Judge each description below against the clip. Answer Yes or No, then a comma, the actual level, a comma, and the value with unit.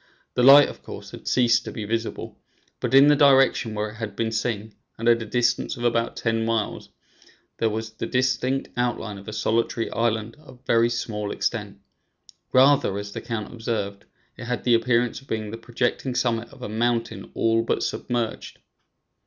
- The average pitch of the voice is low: Yes, low, 115 Hz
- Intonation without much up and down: Yes, narrow, 1.8 semitones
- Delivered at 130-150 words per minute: No, average, 185 wpm